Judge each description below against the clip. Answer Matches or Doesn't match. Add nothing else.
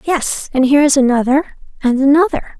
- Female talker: Matches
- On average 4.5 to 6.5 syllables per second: Matches